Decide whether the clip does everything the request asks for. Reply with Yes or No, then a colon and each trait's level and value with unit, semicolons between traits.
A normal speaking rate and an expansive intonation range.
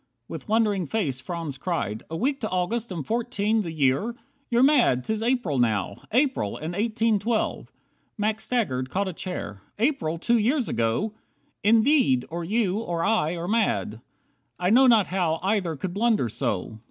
Yes: average, 165 wpm; wide, 6.5 semitones